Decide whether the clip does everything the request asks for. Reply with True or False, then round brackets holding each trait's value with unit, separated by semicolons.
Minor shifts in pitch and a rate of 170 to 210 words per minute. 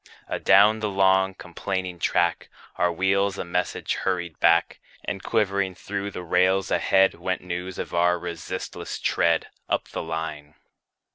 False (1.9 semitones; 140 wpm)